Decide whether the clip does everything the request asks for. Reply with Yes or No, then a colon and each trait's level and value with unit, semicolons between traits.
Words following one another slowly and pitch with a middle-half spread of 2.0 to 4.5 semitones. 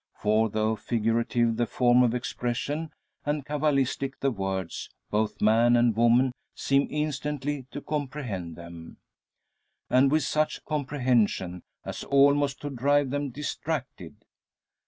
Yes: slow, 120 wpm; average, 4.1 semitones